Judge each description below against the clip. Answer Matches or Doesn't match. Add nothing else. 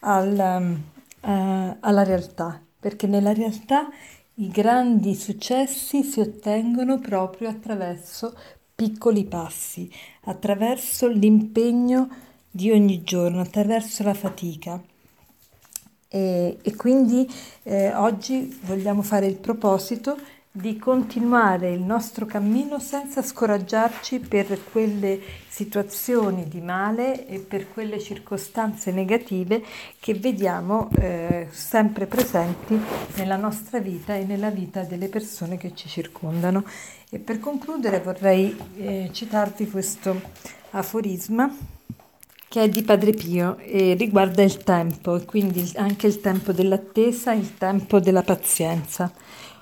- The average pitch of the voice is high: Matches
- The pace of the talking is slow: Matches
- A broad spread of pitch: Doesn't match